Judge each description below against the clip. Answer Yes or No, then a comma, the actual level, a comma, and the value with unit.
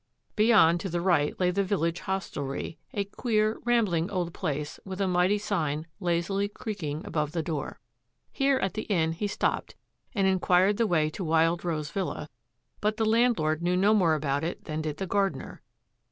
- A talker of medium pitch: Yes, medium, 180 Hz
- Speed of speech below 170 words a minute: No, average, 180 wpm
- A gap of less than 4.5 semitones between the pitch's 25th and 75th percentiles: Yes, average, 4.1 semitones